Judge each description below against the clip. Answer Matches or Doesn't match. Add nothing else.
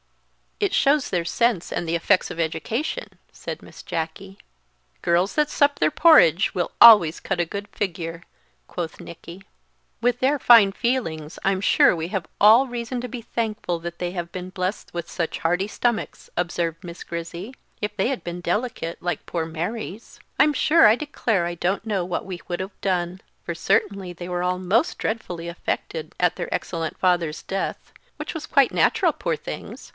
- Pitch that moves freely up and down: Doesn't match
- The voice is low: Doesn't match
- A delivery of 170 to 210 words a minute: Matches